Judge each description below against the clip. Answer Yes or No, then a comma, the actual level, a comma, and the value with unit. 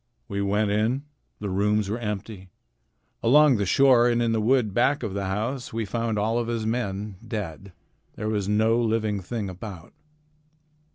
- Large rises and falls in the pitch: No, average, 2.7 semitones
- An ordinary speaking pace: Yes, average, 170 wpm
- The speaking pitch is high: No, low, 110 Hz